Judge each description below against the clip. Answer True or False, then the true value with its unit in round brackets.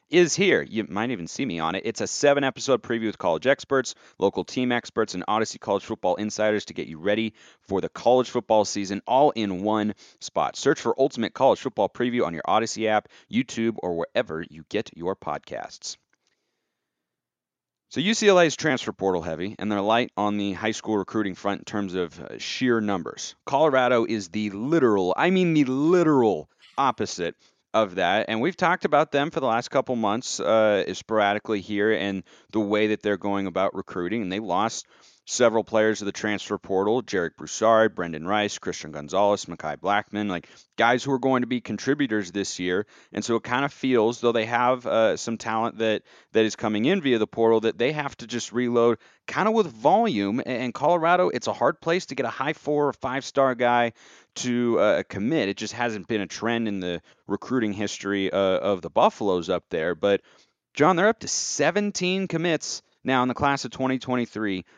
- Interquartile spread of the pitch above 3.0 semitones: True (4.2 semitones)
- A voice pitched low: True (115 Hz)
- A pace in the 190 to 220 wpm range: True (200 wpm)